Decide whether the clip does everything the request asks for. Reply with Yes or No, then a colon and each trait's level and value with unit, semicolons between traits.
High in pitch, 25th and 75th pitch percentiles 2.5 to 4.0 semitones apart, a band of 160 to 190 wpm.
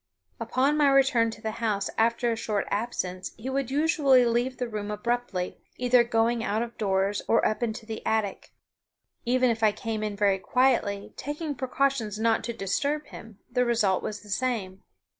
Yes: high, 230 Hz; average, 3.3 semitones; average, 180 wpm